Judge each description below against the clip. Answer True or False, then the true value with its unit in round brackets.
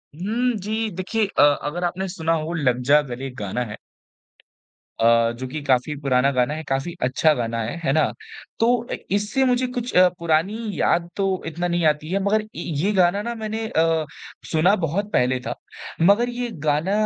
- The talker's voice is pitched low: False (170 Hz)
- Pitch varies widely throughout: True (6.7 semitones)